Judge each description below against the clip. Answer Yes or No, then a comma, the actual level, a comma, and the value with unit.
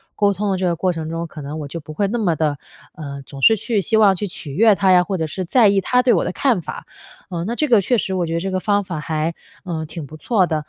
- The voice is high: No, medium, 180 Hz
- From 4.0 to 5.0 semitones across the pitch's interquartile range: Yes, average, 4.3 semitones